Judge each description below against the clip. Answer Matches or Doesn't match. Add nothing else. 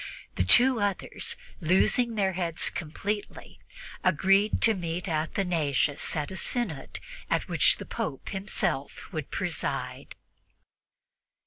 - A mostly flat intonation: Doesn't match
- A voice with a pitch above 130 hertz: Matches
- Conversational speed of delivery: Doesn't match